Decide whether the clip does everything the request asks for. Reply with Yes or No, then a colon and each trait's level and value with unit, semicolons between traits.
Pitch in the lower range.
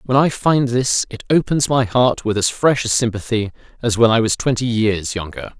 Yes: low, 120 Hz